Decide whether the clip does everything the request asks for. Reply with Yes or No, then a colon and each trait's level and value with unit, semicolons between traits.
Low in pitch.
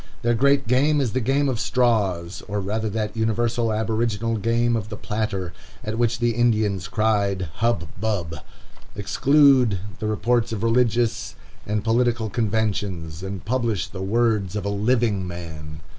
Yes: low, 110 Hz